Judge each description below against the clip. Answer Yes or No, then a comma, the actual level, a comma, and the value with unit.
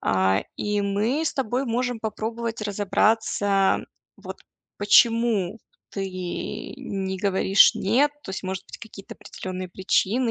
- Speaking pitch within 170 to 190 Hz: No, high, 205 Hz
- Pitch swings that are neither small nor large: Yes, average, 3.3 semitones